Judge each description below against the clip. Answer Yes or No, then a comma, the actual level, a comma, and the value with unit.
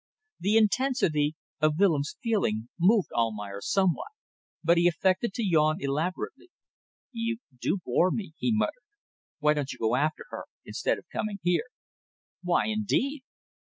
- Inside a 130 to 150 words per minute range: Yes, average, 140 wpm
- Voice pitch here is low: No, medium, 180 Hz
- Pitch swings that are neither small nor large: No, wide, 6.4 semitones